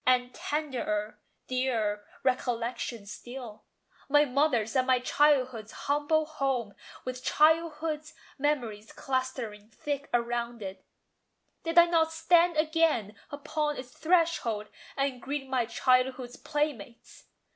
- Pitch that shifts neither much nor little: Yes, average, 4.2 semitones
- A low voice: No, very high, 260 Hz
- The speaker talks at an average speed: No, slow, 110 wpm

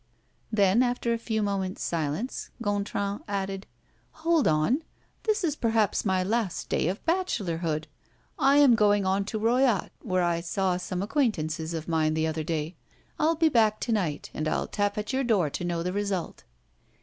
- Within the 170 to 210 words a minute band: Yes, average, 175 wpm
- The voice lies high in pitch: Yes, high, 200 Hz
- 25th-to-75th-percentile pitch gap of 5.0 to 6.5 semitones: Yes, average, 5.3 semitones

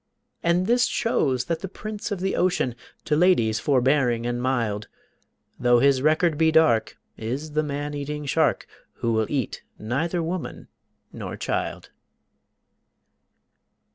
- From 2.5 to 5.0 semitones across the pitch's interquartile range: No, wide, 5.5 semitones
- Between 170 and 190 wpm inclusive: No, slow, 135 wpm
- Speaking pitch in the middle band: Yes, medium, 145 Hz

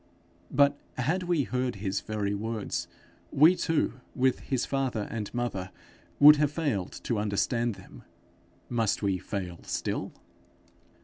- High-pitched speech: No, low, 120 Hz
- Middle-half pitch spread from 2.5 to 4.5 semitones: No, wide, 5.6 semitones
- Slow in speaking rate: Yes, slow, 130 wpm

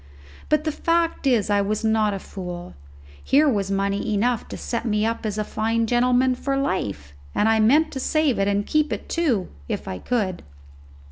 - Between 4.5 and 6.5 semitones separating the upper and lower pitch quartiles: Yes, average, 4.9 semitones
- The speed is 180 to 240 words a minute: Yes, average, 195 wpm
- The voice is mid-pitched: No, high, 225 Hz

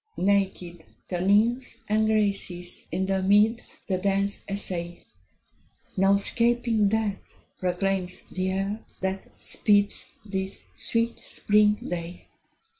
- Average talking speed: No, slow, 110 wpm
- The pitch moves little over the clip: Yes, narrow, 2.1 semitones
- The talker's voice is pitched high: Yes, high, 200 Hz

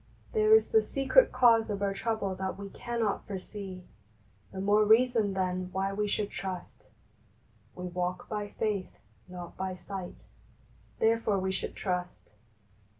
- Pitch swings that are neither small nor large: Yes, average, 3.1 semitones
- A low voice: No, high, 200 Hz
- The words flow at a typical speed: Yes, average, 150 wpm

